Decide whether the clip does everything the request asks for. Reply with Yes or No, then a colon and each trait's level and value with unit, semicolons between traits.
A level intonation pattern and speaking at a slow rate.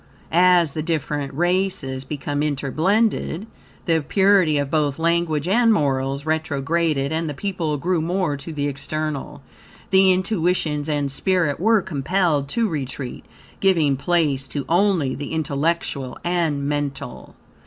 No: average, 3.9 semitones; slow, 130 wpm